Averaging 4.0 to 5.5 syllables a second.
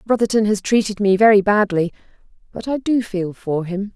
Yes: 5.3 syllables/s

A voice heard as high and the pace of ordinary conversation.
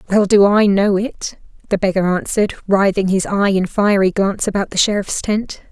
Yes: high, 200 Hz; average, 190 wpm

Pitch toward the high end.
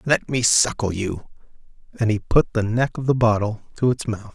No: low, 115 Hz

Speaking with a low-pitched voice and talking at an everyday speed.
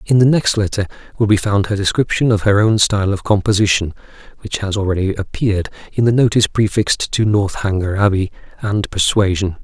Yes: low, 100 Hz; average, 175 wpm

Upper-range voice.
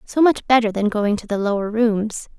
Yes: high, 220 Hz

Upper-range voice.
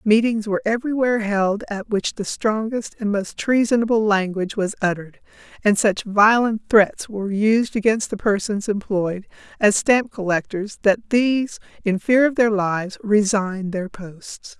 Yes: high, 210 Hz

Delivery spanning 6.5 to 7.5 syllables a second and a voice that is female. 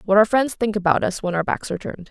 Yes: 7.0 syllables/s; female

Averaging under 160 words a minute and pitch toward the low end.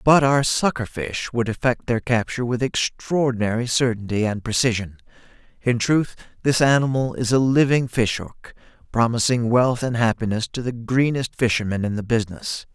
Yes: average, 145 wpm; low, 120 Hz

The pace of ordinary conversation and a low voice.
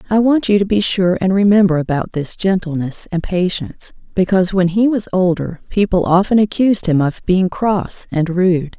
No: average, 185 wpm; medium, 185 Hz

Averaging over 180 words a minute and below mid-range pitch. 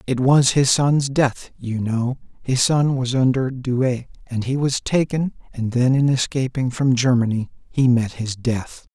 No: average, 175 wpm; low, 130 Hz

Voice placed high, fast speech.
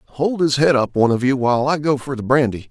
No: low, 135 Hz; fast, 290 wpm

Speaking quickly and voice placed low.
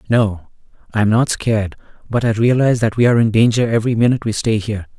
Yes: fast, 215 wpm; low, 110 Hz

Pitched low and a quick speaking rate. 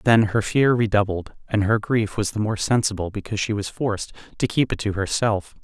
Yes: low, 105 Hz; fast, 215 wpm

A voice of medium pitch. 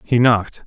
No: low, 115 Hz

